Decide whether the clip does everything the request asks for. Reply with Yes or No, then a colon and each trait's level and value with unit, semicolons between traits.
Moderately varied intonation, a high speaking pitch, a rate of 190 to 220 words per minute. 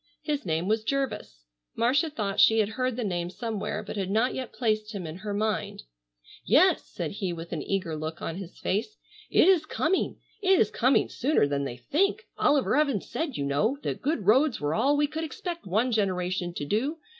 No: wide, 7.1 semitones; high, 215 Hz; average, 200 wpm